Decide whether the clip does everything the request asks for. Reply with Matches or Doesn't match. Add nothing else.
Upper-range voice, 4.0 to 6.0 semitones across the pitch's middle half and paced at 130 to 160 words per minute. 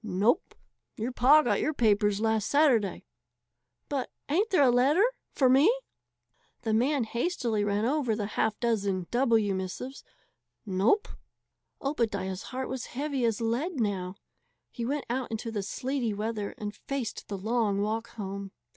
Matches